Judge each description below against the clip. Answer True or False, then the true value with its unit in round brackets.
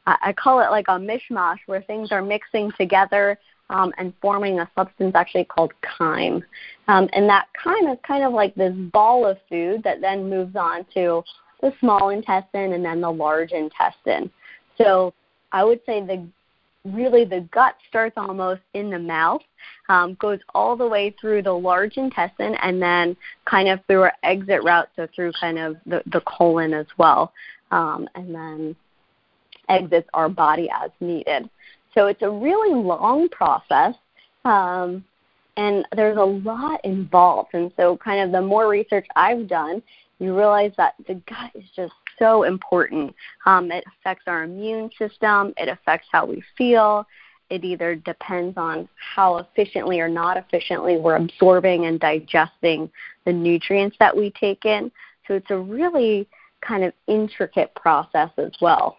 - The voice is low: False (190 Hz)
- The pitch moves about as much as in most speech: True (3.2 semitones)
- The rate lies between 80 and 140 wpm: False (165 wpm)